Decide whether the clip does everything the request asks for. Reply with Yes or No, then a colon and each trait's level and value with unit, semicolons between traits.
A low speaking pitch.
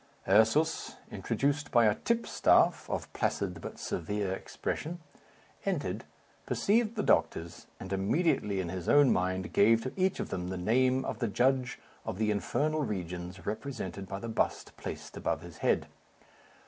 Yes: low, 110 Hz